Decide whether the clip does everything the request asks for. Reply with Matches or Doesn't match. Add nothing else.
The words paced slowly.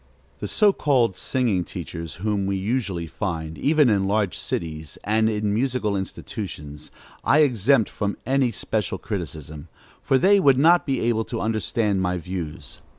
Doesn't match